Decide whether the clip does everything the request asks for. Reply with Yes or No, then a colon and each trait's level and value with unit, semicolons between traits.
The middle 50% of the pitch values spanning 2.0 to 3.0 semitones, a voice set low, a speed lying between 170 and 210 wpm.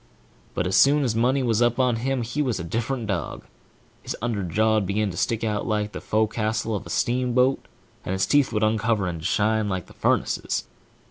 Yes: average, 2.7 semitones; low, 110 Hz; fast, 205 wpm